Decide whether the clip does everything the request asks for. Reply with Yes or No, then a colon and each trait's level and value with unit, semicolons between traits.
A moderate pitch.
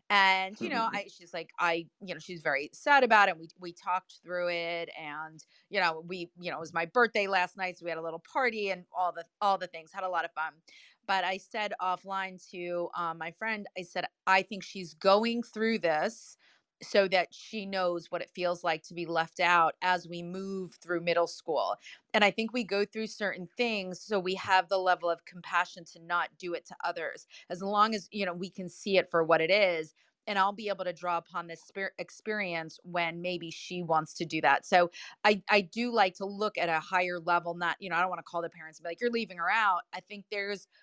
Yes: medium, 180 Hz